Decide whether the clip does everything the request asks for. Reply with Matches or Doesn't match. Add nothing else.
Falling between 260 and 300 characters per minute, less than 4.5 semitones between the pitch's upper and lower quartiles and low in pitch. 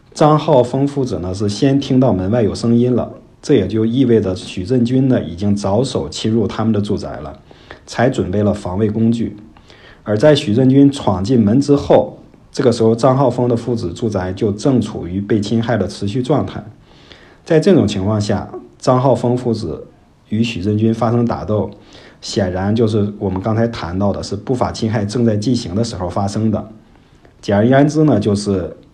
Matches